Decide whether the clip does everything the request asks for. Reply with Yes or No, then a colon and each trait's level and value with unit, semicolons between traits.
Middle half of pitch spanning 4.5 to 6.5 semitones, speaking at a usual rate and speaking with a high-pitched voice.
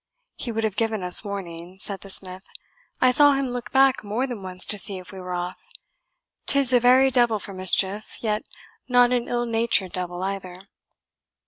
Yes: average, 4.8 semitones; average, 190 wpm; high, 210 Hz